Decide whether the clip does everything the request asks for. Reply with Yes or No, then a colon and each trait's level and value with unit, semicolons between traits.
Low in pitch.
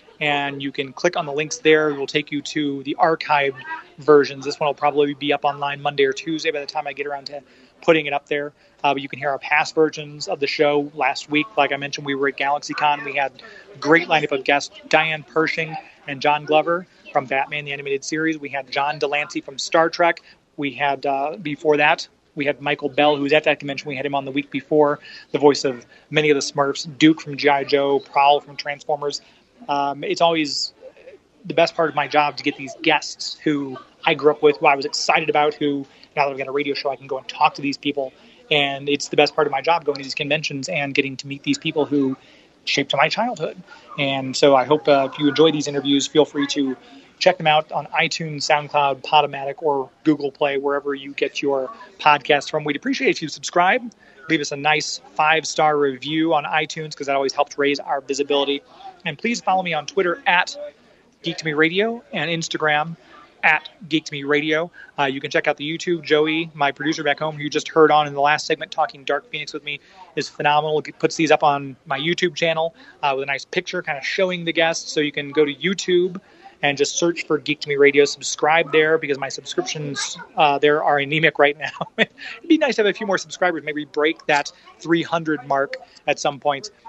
No: medium, 150 Hz